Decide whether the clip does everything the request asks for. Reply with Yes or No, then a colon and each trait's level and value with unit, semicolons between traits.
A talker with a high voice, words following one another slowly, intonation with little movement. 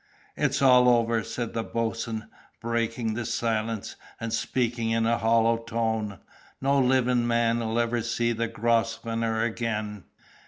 No: low, 115 Hz; slow, 130 wpm; narrow, 0.8 semitones